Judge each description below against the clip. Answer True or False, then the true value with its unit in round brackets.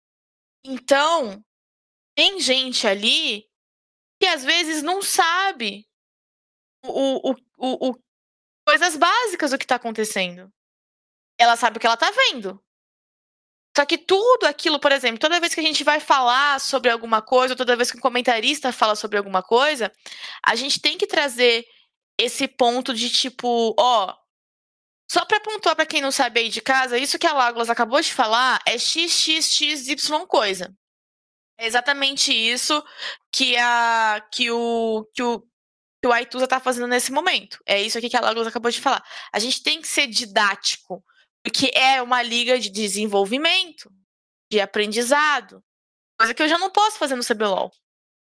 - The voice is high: True (255 Hz)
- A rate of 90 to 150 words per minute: False (165 wpm)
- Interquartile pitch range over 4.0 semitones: True (4.6 semitones)